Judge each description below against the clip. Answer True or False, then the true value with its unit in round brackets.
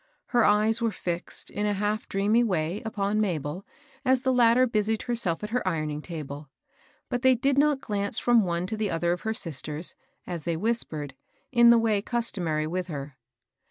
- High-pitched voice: True (205 Hz)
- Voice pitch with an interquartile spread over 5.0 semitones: True (5.6 semitones)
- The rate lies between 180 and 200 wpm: True (185 wpm)